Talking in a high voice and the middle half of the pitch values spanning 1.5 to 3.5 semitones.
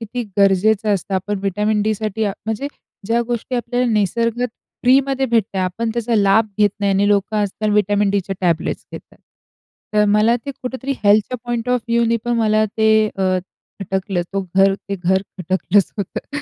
Yes: high, 210 Hz; average, 2.9 semitones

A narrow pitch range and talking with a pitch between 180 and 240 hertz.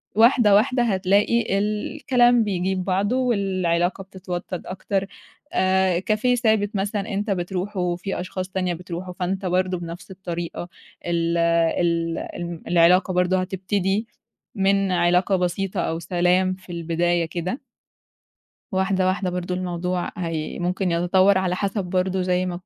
Yes: narrow, 2.0 semitones; medium, 185 Hz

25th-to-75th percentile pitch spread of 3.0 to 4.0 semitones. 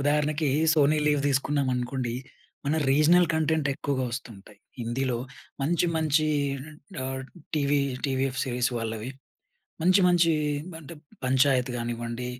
Yes: average, 3.4 semitones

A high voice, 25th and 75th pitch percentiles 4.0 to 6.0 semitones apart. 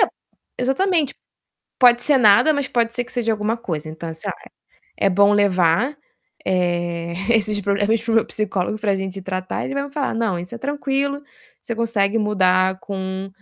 Yes: high, 210 Hz; average, 4.4 semitones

